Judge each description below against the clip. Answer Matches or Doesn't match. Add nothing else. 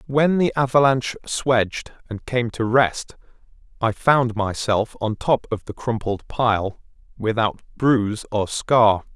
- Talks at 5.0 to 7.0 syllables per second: Doesn't match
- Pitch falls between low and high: Doesn't match